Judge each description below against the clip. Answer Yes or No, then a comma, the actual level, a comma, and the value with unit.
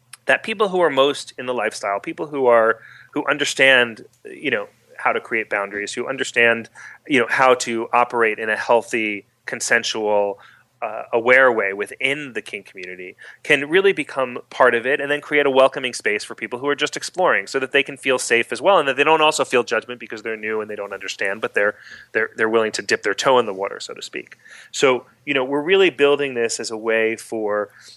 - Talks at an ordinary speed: No, fast, 220 wpm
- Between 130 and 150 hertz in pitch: No, low, 120 Hz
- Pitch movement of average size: Yes, average, 4.2 semitones